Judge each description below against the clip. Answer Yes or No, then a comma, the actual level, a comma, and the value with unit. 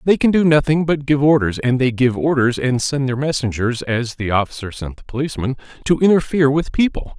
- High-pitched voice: No, low, 135 Hz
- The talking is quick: Yes, fast, 210 wpm